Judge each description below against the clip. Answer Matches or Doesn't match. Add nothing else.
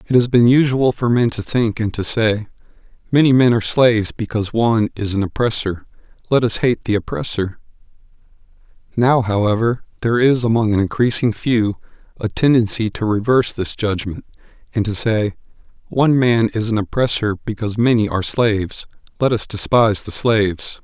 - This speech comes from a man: Matches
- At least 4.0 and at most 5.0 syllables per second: Doesn't match